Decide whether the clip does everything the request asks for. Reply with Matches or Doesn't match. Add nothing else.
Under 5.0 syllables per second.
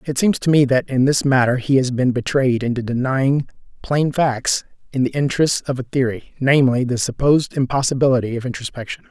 Doesn't match